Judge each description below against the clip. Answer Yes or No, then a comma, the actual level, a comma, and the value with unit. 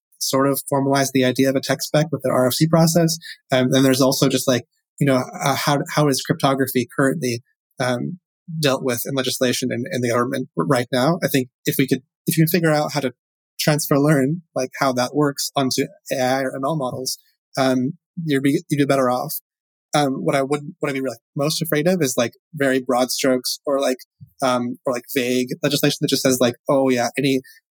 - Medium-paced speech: No, fast, 215 wpm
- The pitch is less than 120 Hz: No, low, 135 Hz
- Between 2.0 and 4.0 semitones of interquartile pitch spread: Yes, narrow, 2.4 semitones